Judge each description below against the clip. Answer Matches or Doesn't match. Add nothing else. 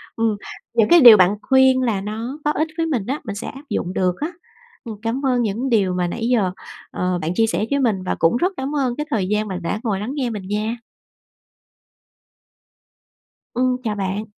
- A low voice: Doesn't match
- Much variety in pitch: Doesn't match